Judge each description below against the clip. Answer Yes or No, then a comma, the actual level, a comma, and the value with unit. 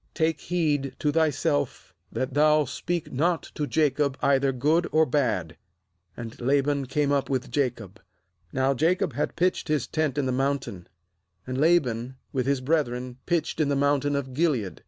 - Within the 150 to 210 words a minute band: Yes, average, 160 wpm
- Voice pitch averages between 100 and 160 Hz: Yes, medium, 140 Hz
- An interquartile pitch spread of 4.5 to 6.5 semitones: No, average, 3.1 semitones